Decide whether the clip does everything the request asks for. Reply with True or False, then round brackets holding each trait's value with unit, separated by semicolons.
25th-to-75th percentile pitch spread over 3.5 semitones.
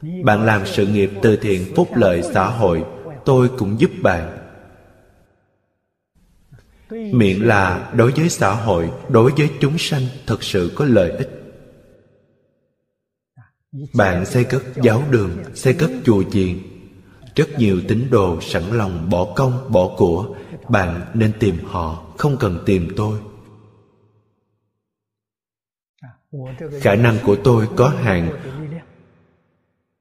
True (4.7 semitones)